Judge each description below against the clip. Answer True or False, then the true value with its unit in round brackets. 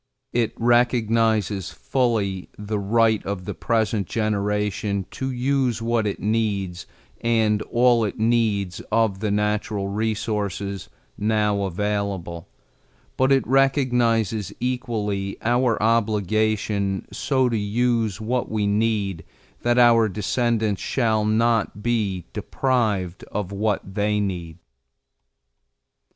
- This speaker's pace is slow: True (110 wpm)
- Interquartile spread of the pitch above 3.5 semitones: False (2.5 semitones)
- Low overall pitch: True (110 Hz)